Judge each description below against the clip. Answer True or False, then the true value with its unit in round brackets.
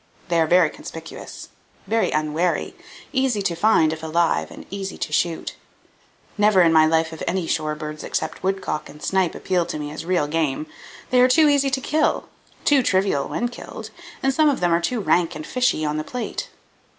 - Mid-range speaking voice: True (175 Hz)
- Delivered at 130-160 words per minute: False (195 wpm)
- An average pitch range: False (5.9 semitones)